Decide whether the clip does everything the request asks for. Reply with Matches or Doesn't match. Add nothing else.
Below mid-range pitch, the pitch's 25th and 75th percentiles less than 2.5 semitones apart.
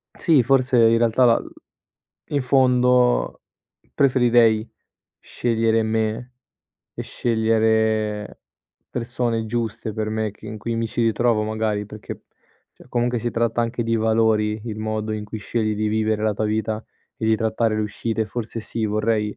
Matches